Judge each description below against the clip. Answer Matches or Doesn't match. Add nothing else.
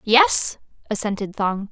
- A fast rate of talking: Doesn't match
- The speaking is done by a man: Doesn't match